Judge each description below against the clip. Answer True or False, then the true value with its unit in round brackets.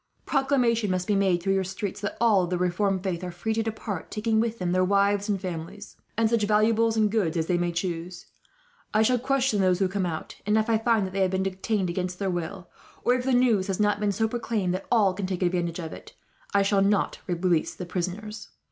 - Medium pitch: False (195 Hz)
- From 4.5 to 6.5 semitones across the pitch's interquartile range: False (3.2 semitones)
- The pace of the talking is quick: True (235 wpm)